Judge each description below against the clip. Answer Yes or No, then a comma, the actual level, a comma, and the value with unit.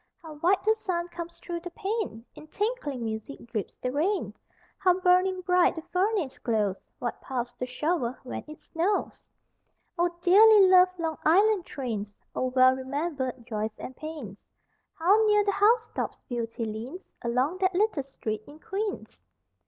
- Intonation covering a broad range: Yes, wide, 7.0 semitones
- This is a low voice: No, very high, 325 Hz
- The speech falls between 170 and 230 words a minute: No, average, 155 wpm